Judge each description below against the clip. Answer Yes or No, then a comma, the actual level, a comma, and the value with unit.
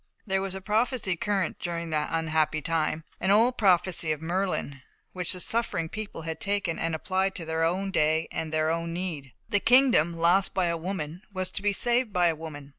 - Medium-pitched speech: Yes, medium, 175 Hz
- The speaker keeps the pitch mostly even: No, average, 3.3 semitones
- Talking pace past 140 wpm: Yes, average, 200 wpm